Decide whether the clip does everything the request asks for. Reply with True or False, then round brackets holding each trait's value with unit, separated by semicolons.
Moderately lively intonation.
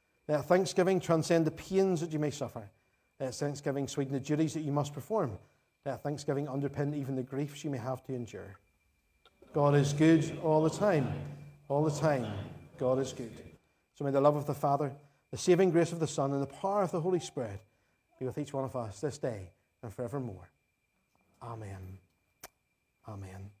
True (4.4 semitones)